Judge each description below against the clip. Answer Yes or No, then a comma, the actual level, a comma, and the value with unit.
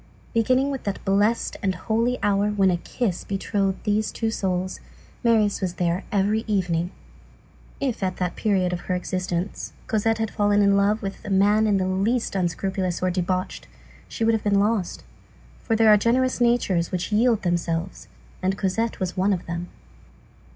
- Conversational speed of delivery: Yes, average, 170 wpm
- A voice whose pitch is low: No, high, 200 Hz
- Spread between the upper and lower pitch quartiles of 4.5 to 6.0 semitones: No, average, 3.1 semitones